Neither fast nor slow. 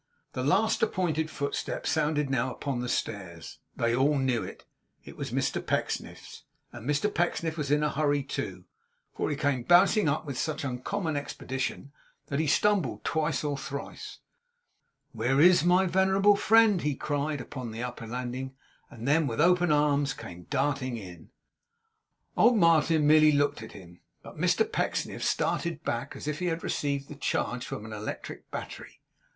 Yes: average, 165 wpm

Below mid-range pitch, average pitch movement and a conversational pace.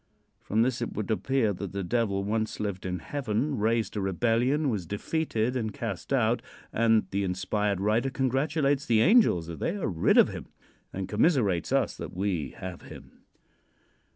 Yes: low, 110 Hz; average, 4.8 semitones; average, 170 wpm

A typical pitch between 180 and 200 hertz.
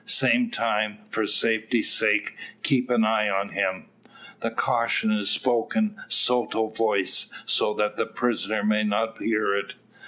No: low, 110 Hz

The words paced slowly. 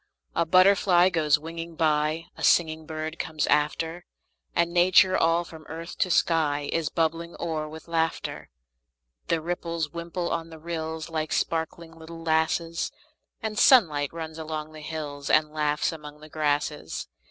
No: average, 150 wpm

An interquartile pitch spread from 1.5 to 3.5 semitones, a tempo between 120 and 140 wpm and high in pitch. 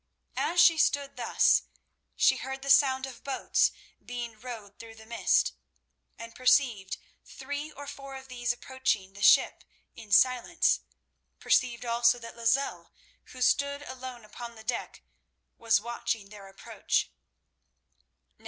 Yes: average, 2.8 semitones; slow, 135 wpm; high, 245 Hz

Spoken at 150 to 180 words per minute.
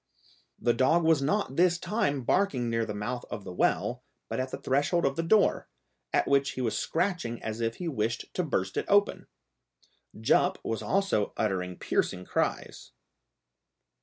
Yes: average, 165 wpm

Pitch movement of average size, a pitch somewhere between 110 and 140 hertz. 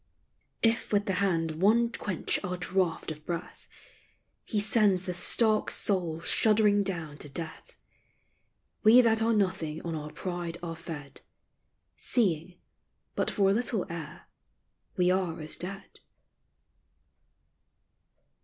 No: average, 4.0 semitones; medium, 185 Hz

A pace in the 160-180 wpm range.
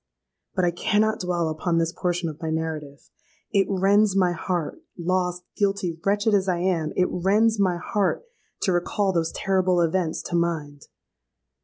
No: average, 150 wpm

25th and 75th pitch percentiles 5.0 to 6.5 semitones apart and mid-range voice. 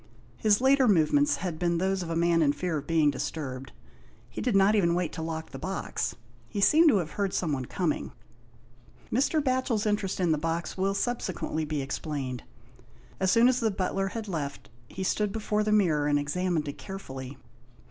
Yes: average, 5.3 semitones; medium, 180 Hz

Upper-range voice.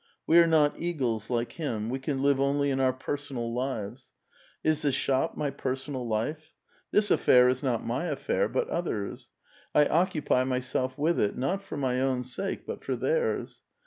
No: low, 135 Hz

